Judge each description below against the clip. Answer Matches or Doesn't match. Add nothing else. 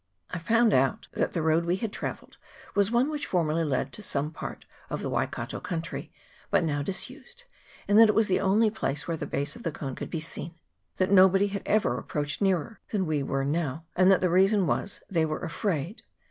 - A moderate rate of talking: Doesn't match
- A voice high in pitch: Doesn't match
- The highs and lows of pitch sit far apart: Doesn't match